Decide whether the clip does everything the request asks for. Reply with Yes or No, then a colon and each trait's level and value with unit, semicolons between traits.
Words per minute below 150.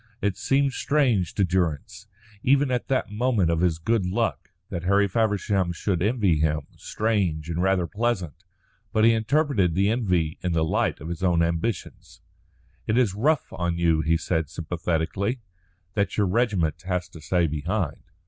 No: average, 165 wpm